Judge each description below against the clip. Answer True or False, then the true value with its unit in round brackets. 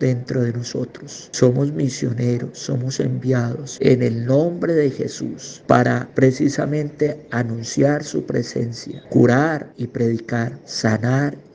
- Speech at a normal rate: False (110 wpm)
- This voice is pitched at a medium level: False (125 Hz)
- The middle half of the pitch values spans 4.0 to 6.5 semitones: False (3.0 semitones)